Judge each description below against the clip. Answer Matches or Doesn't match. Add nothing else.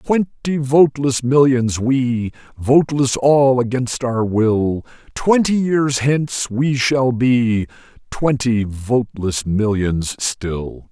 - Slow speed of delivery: Matches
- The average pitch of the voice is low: Matches